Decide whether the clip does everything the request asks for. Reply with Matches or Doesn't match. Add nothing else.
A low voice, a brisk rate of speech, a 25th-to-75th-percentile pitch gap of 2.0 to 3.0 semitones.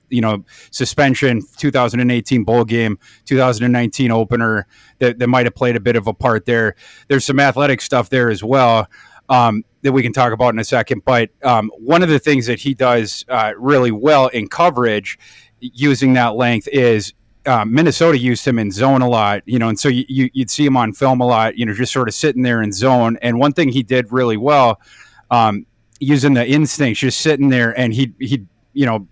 Matches